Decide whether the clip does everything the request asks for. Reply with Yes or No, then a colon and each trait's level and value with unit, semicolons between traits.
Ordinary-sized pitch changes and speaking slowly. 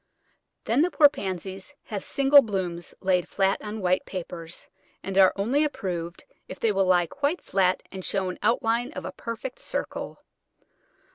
No: average, 4.2 semitones; average, 160 wpm